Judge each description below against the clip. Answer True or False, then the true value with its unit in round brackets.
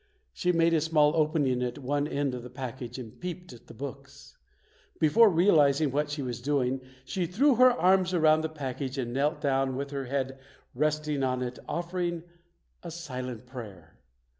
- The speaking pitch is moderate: True (145 Hz)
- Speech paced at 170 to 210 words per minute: True (180 wpm)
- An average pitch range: True (4.1 semitones)